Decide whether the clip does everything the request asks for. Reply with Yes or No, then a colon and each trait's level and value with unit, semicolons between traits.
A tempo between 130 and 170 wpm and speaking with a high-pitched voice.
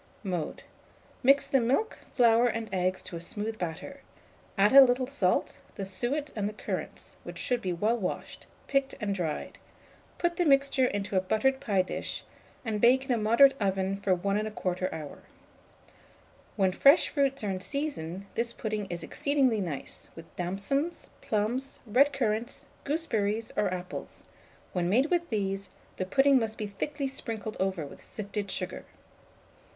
Yes: average, 160 wpm; high, 215 Hz